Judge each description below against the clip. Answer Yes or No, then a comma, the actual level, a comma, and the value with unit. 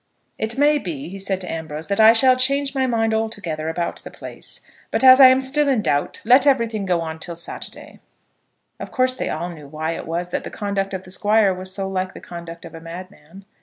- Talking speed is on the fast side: Yes, fast, 230 wpm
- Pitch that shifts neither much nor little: No, wide, 6.4 semitones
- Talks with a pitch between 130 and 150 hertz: No, high, 195 Hz